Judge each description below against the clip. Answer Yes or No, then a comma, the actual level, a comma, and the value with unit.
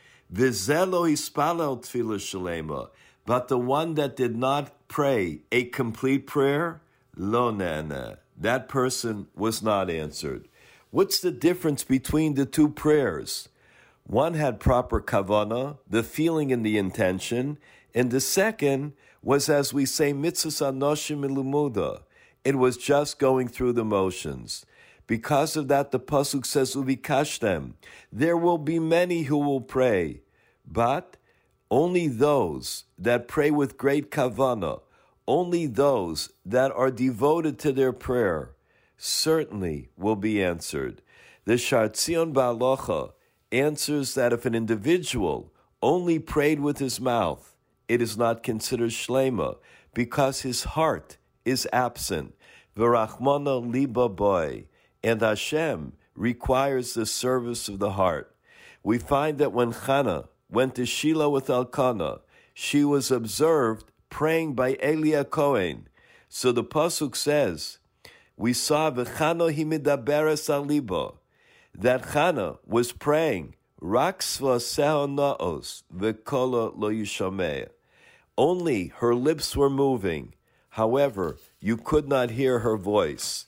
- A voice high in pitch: No, low, 135 Hz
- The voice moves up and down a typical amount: Yes, average, 3.8 semitones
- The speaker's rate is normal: No, slow, 115 wpm